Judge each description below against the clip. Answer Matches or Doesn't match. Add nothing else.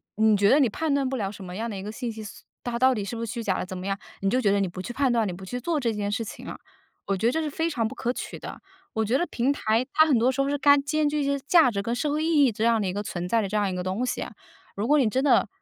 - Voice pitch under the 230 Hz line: Doesn't match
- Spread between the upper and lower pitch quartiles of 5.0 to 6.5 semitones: Matches